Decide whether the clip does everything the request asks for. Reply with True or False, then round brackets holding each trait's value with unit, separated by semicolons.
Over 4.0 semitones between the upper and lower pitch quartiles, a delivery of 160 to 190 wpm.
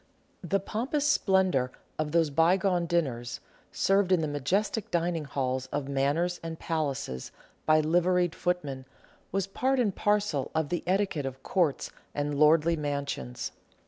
False (4.7 semitones; 140 wpm)